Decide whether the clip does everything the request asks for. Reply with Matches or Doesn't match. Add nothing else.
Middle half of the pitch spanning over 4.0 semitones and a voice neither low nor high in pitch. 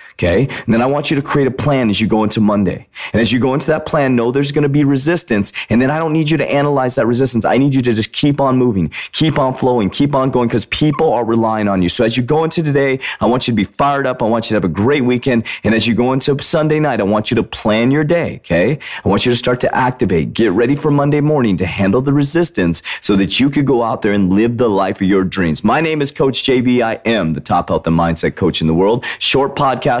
Doesn't match